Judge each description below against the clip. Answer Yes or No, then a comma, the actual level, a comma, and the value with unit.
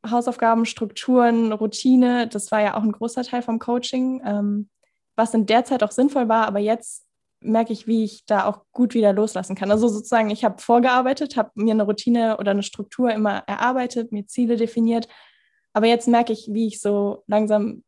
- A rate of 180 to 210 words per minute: Yes, fast, 190 wpm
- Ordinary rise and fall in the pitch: No, narrow, 2.1 semitones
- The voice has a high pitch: Yes, high, 225 Hz